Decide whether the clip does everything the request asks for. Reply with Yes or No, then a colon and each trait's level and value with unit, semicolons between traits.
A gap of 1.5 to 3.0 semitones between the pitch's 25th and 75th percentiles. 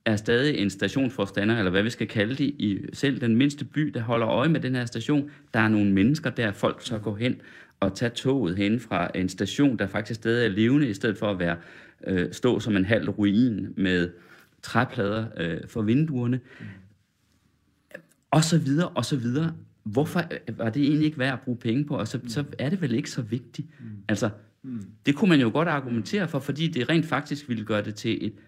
No: average, 5.1 semitones